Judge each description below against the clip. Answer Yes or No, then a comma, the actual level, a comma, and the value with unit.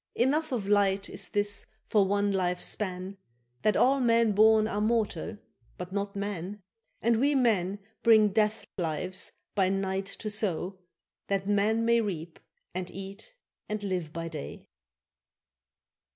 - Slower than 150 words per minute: Yes, average, 140 wpm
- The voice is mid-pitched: No, high, 205 Hz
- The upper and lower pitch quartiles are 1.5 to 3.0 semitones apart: Yes, narrow, 2.6 semitones